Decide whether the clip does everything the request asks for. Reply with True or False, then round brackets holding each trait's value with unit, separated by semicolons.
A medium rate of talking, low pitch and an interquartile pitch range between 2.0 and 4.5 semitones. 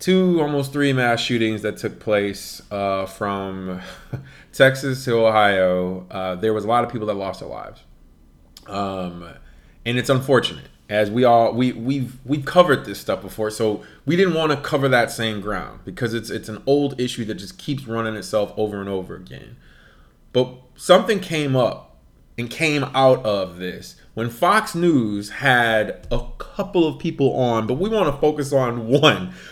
False (175 wpm; 115 Hz; 5.5 semitones)